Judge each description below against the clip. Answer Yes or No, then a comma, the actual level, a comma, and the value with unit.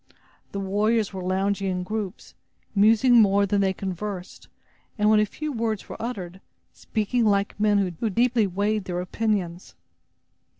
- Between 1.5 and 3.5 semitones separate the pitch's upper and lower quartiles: Yes, narrow, 2.4 semitones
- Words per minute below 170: Yes, average, 145 wpm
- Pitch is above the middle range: Yes, high, 205 Hz